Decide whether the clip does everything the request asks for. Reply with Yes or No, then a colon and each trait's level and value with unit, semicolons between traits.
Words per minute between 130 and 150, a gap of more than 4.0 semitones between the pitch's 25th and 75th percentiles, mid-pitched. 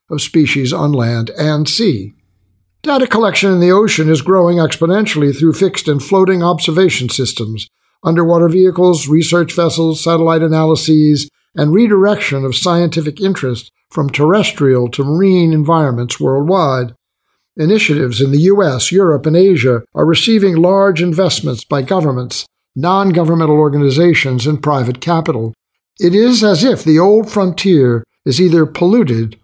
Yes: slow, 135 wpm; average, 5.0 semitones; medium, 160 Hz